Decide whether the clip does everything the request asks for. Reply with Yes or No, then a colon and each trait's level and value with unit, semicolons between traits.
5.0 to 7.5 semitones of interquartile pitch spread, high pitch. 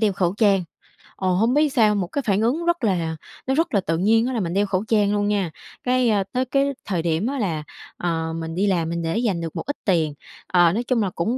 Yes: average, 5.3 semitones; high, 200 Hz